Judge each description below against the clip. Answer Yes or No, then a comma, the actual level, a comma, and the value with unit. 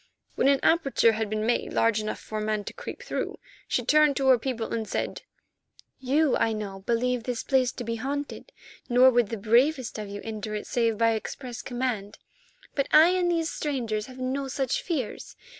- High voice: Yes, high, 245 Hz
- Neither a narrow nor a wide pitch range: Yes, average, 3.8 semitones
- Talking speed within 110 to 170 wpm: No, average, 195 wpm